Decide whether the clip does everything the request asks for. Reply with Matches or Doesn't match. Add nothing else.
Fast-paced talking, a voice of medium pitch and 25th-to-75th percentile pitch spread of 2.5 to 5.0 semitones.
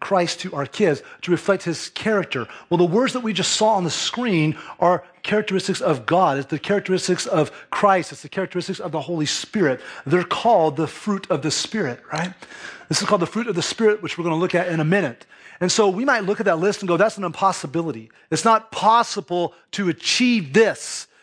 Matches